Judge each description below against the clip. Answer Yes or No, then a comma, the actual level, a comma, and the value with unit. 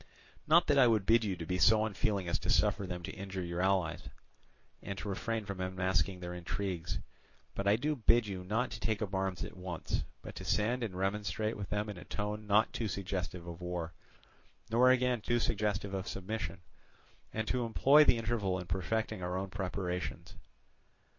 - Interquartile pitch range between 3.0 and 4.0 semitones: Yes, average, 3.3 semitones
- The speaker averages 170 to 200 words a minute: Yes, average, 190 wpm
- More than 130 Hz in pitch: No, low, 100 Hz